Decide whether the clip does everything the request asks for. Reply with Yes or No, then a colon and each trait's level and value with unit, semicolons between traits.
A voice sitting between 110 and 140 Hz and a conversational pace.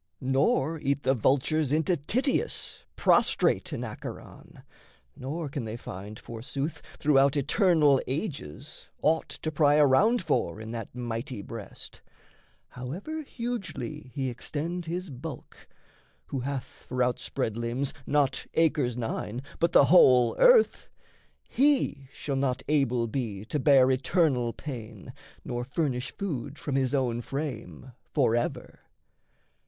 No: low, 135 Hz; slow, 125 wpm